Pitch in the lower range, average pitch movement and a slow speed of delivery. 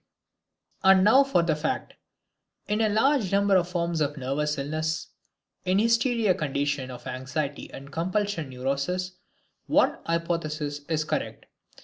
No: medium, 165 Hz; average, 5.0 semitones; slow, 130 wpm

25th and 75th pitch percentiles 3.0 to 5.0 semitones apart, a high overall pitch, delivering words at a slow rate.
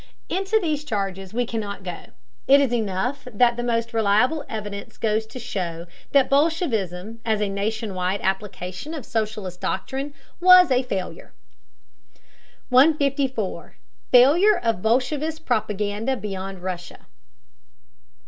No: wide, 5.5 semitones; high, 225 Hz; slow, 120 wpm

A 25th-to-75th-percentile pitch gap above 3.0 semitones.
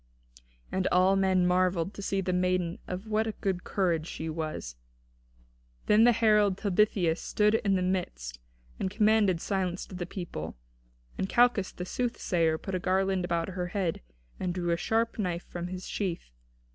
No: narrow, 2.4 semitones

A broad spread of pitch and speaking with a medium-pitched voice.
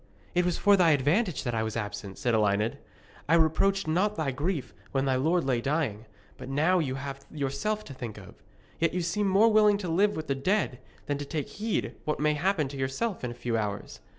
Yes: wide, 5.9 semitones; medium, 150 Hz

